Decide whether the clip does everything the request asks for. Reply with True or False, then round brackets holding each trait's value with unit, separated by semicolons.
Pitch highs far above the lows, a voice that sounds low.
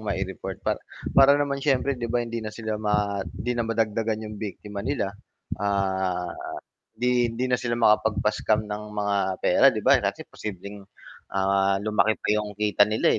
False (2.5 semitones; 105 Hz)